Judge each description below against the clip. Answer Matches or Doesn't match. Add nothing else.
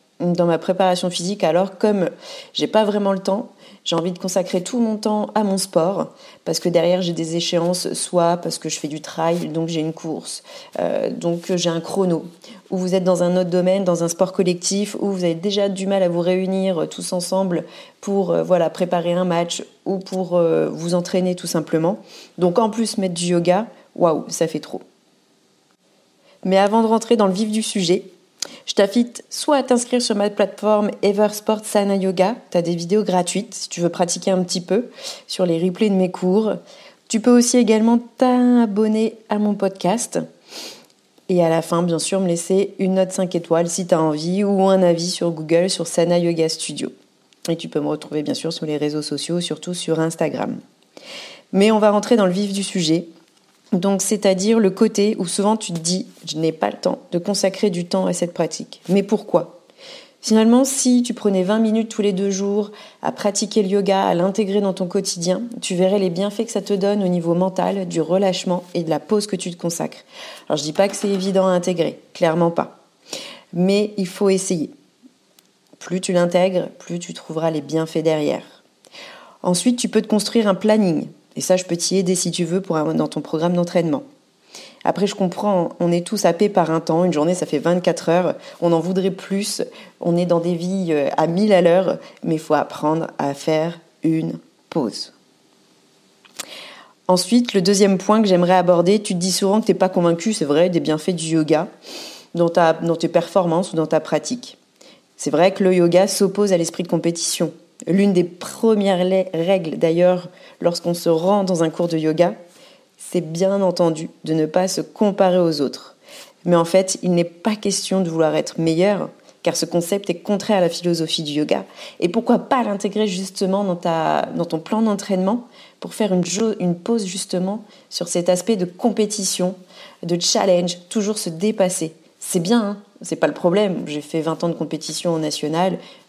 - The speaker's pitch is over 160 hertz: Matches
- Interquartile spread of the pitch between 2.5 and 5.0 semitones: Matches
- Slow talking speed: Doesn't match